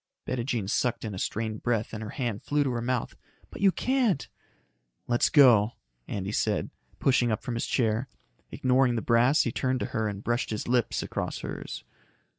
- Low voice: Yes, low, 120 Hz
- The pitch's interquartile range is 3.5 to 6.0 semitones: No, average, 2.8 semitones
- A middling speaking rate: Yes, average, 190 wpm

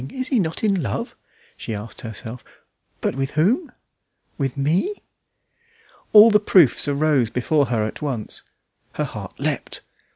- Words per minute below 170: Yes, average, 140 wpm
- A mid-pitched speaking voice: Yes, medium, 145 Hz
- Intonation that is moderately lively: No, wide, 8.3 semitones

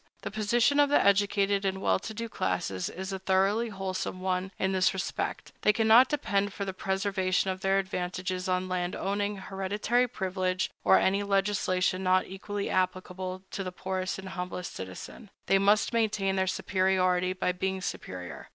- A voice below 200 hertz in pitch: Yes, high, 190 Hz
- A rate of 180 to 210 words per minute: No, average, 170 wpm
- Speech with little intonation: Yes, narrow, 1.6 semitones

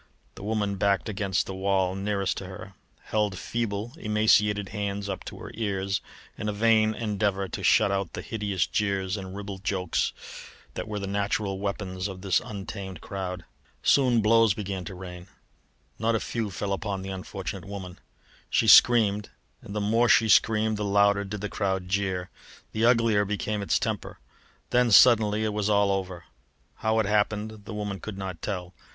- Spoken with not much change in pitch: Yes, narrow, 1.8 semitones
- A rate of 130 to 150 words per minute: No, average, 175 wpm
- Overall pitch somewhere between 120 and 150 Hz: No, low, 100 Hz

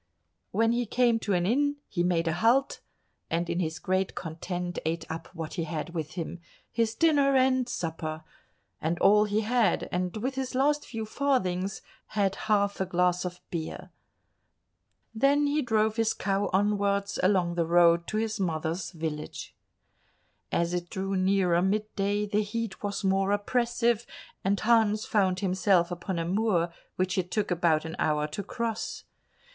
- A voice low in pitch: No, high, 195 Hz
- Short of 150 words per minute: No, average, 160 wpm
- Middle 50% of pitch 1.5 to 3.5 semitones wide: No, average, 4.3 semitones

